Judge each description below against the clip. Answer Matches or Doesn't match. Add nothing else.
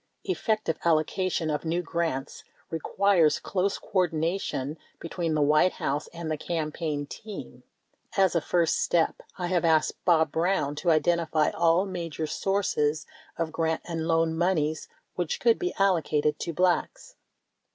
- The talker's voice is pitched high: Doesn't match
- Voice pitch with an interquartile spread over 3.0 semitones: Doesn't match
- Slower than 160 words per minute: Matches